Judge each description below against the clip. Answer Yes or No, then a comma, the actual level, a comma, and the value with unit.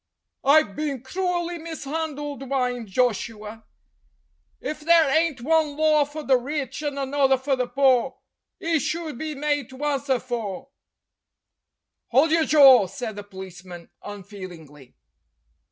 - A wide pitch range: No, average, 4.7 semitones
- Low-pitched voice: No, very high, 270 Hz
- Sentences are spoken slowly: Yes, slow, 130 wpm